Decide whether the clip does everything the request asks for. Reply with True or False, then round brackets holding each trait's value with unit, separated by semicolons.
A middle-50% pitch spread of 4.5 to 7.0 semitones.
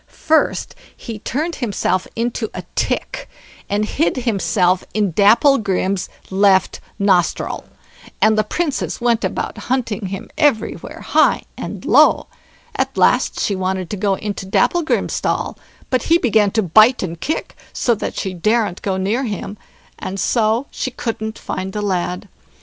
False (3.7 semitones)